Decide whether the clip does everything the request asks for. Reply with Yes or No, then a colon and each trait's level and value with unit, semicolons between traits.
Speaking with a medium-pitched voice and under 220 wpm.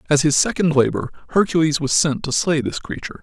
Yes: medium, 150 Hz; fast, 205 wpm